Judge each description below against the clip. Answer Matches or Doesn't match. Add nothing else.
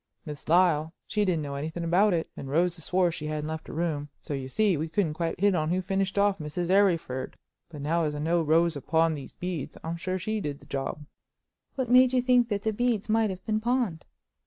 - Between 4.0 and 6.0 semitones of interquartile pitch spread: Matches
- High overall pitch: Doesn't match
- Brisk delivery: Matches